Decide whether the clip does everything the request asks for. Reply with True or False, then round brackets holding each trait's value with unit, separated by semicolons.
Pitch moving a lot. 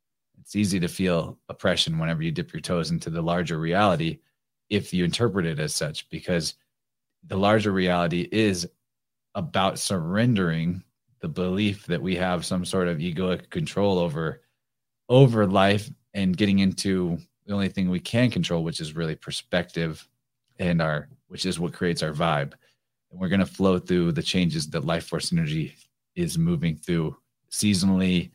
True (5.9 semitones)